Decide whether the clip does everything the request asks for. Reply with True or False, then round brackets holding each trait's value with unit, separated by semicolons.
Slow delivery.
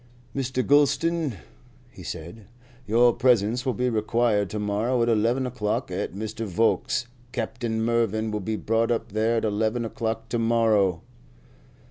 False (145 wpm)